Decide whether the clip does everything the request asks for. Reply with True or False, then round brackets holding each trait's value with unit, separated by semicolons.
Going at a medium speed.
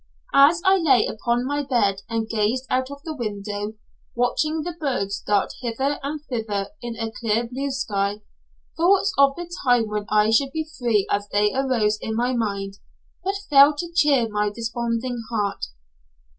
True (170 wpm)